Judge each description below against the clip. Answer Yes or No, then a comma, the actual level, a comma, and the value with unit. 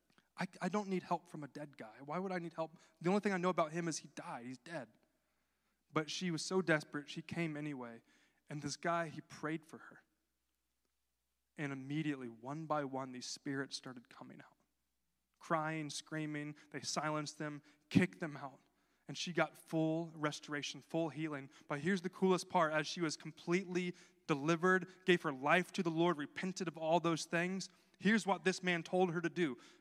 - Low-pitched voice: No, medium, 160 Hz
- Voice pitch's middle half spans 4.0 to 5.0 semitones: No, average, 3.4 semitones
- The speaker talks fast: No, average, 190 wpm